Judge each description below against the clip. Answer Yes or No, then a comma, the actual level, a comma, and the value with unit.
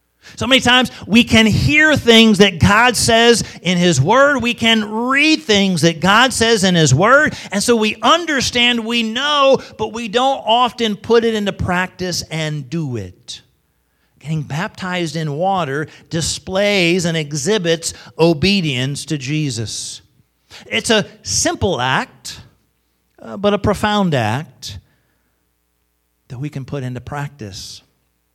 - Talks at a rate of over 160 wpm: No, slow, 135 wpm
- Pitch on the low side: No, medium, 180 Hz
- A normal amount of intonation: No, wide, 8.8 semitones